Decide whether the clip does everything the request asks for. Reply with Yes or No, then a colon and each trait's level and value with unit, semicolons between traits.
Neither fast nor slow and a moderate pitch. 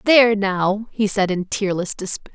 No: average, 180 wpm; high, 200 Hz